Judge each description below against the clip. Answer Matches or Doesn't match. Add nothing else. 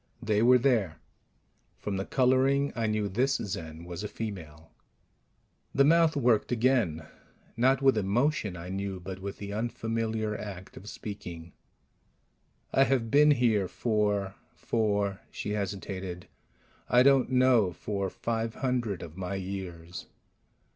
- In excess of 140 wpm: Doesn't match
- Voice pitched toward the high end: Doesn't match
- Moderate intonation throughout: Matches